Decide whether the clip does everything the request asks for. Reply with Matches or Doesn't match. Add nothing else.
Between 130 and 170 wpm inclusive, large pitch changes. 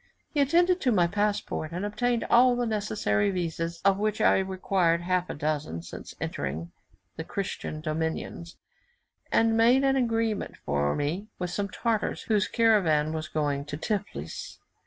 Matches